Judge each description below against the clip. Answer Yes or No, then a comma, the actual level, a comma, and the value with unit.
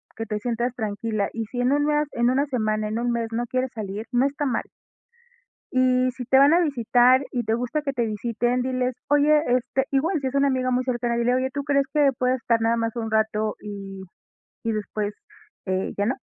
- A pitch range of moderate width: Yes, average, 3.0 semitones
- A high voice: Yes, high, 245 Hz